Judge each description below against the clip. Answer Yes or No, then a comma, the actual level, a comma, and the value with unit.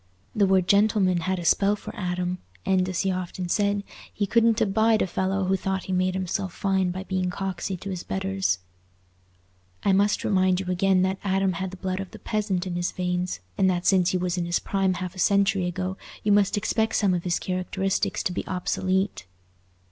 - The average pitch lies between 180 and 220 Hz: Yes, high, 190 Hz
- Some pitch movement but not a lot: No, narrow, 1.3 semitones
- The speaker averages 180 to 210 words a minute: Yes, average, 200 wpm